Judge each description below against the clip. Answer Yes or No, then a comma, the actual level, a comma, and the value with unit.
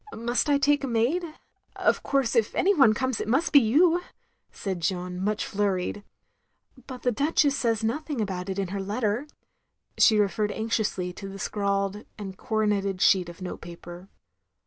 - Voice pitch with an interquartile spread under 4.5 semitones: No, average, 4.8 semitones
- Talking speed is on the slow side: No, average, 170 wpm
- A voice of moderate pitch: No, high, 215 Hz